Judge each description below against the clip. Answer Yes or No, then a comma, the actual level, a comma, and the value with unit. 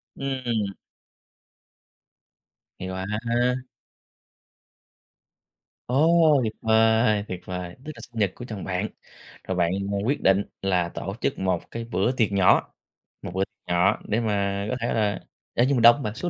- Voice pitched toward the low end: Yes, low, 105 Hz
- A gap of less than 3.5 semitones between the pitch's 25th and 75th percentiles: No, average, 3.9 semitones